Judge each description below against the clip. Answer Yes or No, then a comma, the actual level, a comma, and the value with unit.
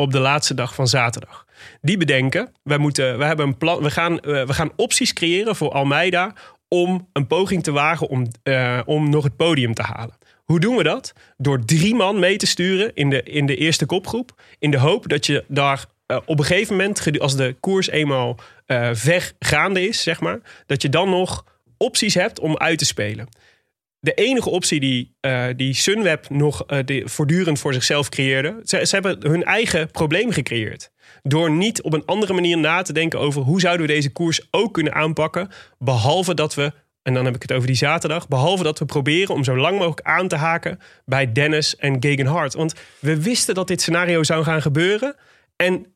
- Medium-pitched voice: Yes, medium, 155 Hz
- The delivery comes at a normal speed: No, fast, 205 wpm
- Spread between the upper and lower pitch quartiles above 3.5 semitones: Yes, average, 4.2 semitones